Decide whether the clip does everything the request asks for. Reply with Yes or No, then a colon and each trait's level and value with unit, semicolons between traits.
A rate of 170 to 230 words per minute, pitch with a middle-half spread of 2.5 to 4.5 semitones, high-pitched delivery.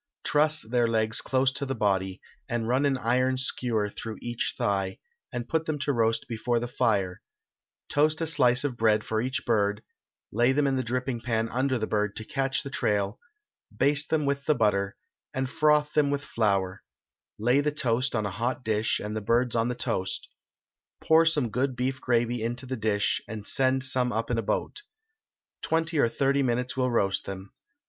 No: average, 190 wpm; average, 3.6 semitones; low, 120 Hz